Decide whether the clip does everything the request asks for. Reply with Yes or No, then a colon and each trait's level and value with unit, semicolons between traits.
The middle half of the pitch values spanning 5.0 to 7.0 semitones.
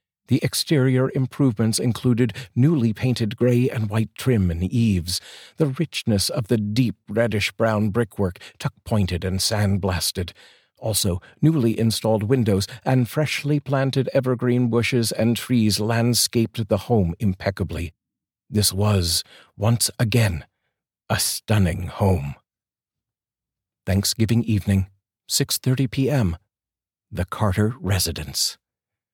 No: average, 3.8 semitones